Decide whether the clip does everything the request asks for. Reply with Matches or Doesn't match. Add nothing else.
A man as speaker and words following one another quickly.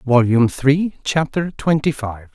Doesn't match